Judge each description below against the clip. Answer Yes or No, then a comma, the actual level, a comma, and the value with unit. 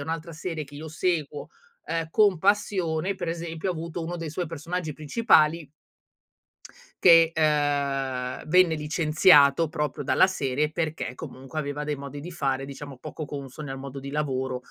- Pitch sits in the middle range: Yes, medium, 155 Hz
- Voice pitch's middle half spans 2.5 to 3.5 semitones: Yes, average, 2.9 semitones